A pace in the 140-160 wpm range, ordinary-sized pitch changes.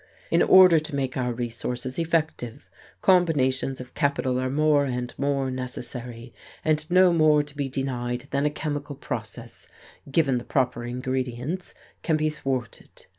Yes: average, 145 wpm; average, 3.4 semitones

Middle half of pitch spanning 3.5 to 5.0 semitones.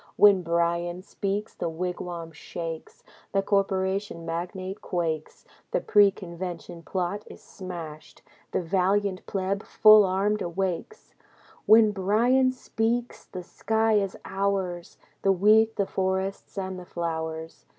No: average, 2.9 semitones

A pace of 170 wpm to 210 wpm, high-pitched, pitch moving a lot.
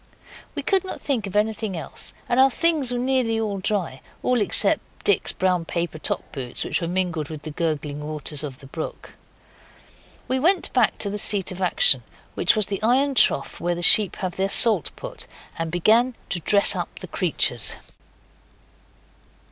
Yes: average, 175 wpm; high, 195 Hz; wide, 6.7 semitones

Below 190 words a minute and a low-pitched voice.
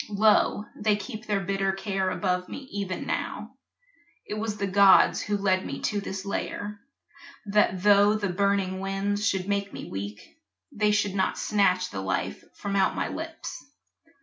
No: average, 165 wpm; high, 200 Hz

